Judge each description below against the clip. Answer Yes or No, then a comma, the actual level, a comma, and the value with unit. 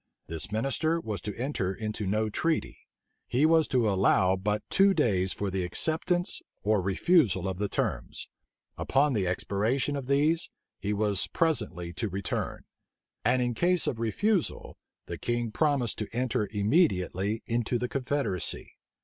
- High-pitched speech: No, low, 115 Hz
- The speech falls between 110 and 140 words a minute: No, average, 150 wpm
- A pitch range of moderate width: No, wide, 6.3 semitones